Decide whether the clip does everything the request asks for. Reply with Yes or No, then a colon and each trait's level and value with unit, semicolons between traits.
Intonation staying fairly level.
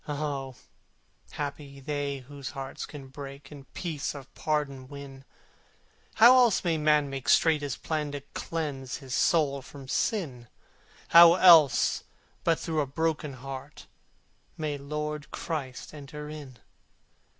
Yes: narrow, 2.1 semitones